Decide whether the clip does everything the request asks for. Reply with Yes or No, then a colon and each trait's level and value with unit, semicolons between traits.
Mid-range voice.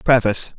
No: low, 115 Hz